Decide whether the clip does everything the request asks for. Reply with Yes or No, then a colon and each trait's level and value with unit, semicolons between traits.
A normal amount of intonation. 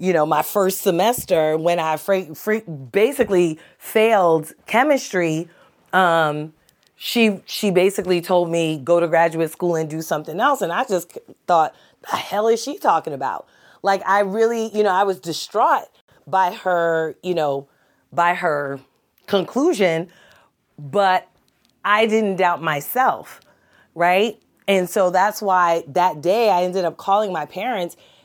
Yes: average, 3.6 semitones